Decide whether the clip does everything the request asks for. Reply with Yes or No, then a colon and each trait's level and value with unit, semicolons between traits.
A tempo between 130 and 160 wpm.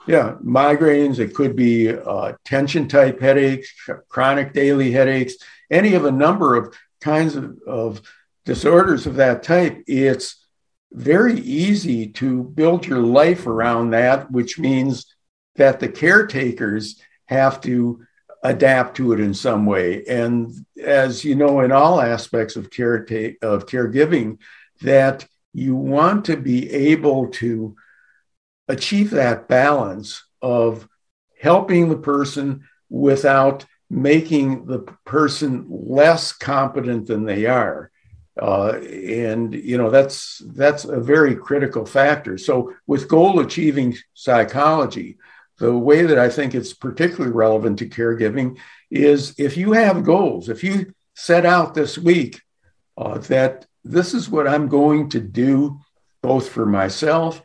Yes: slow, 135 wpm